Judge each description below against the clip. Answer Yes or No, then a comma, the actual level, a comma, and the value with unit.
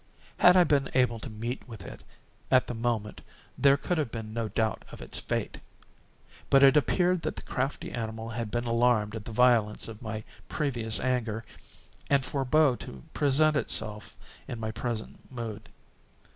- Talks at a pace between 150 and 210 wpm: Yes, average, 170 wpm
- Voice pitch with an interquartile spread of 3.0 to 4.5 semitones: Yes, average, 3.7 semitones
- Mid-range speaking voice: No, low, 120 Hz